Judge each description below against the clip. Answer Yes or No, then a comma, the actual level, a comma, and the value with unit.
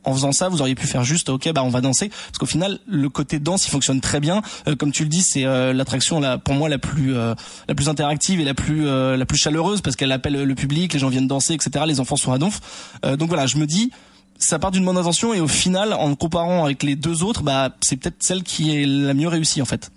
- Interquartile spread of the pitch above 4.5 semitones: No, average, 3.9 semitones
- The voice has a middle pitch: Yes, medium, 150 Hz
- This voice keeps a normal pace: No, fast, 285 wpm